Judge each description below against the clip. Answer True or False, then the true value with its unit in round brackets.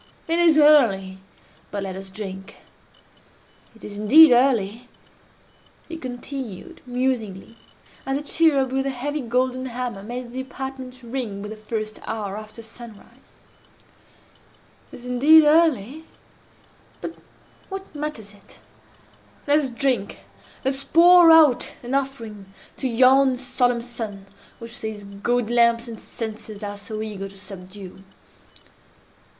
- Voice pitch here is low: False (245 Hz)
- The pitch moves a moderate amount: True (4.3 semitones)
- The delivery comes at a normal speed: False (125 wpm)